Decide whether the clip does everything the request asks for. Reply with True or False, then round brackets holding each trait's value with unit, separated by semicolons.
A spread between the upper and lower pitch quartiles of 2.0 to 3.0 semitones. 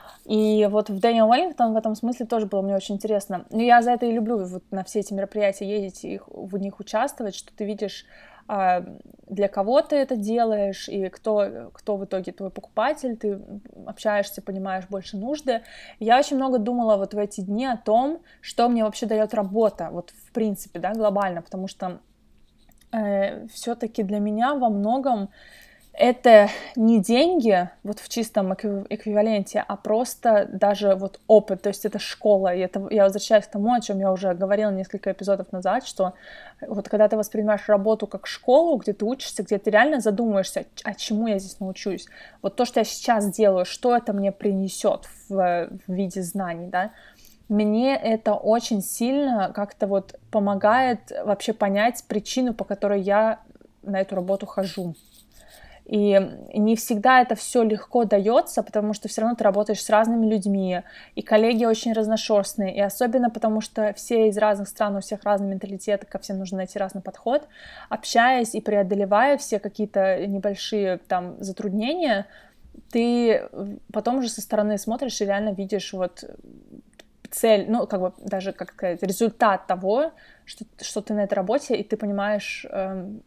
True (2.5 semitones)